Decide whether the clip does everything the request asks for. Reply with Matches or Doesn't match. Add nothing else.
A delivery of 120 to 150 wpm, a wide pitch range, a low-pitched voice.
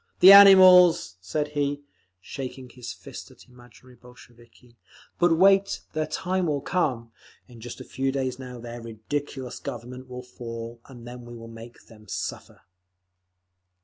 Doesn't match